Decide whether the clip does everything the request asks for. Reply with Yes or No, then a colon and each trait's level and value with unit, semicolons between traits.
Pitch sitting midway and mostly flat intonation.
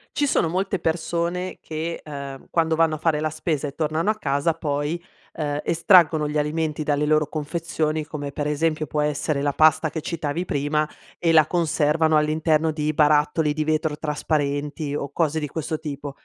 Yes: medium, 155 Hz; narrow, 1.6 semitones